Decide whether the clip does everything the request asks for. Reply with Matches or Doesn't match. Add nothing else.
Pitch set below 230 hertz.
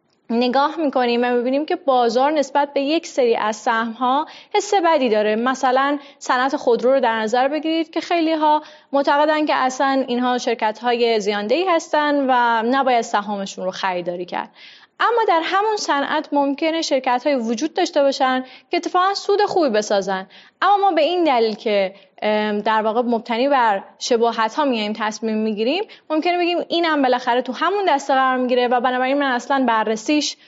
Doesn't match